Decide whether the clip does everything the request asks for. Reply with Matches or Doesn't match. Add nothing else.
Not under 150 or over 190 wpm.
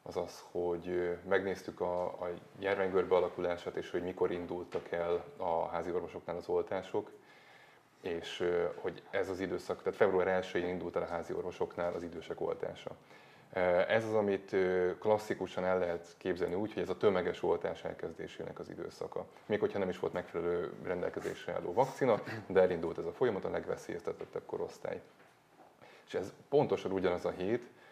Matches